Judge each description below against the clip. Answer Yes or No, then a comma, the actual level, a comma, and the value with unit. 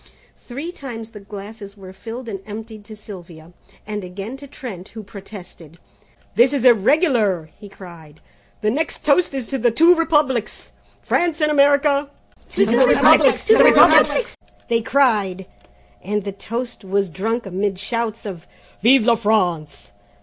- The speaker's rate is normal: Yes, average, 150 wpm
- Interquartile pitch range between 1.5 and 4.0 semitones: No, average, 5.1 semitones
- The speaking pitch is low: No, high, 220 Hz